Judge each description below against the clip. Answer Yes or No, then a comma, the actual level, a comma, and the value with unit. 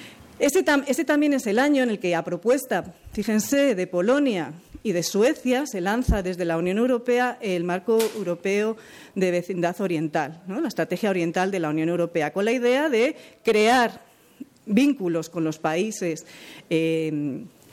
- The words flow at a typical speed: Yes, average, 160 wpm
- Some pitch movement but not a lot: No, wide, 6.1 semitones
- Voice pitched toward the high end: Yes, high, 195 Hz